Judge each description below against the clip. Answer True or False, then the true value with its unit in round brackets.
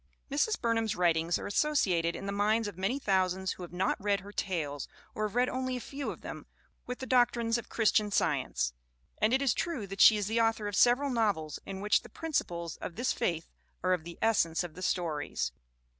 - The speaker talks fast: True (220 wpm)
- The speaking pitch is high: True (205 Hz)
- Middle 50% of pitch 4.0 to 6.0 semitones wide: True (5.0 semitones)